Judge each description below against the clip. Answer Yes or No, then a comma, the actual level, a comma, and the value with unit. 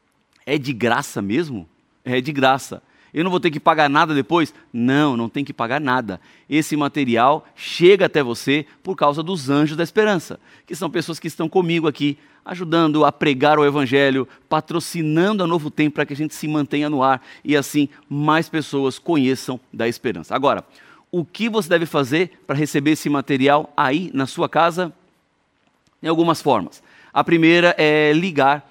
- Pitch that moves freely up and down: No, average, 3.0 semitones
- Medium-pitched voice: Yes, medium, 150 Hz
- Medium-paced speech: Yes, average, 175 wpm